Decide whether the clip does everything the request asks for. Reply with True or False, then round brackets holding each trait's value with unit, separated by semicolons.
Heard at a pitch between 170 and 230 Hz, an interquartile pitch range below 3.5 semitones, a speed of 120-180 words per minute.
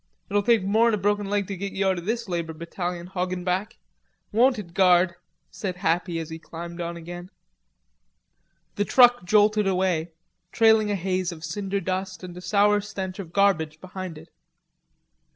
True (185 Hz; 2.8 semitones; 170 wpm)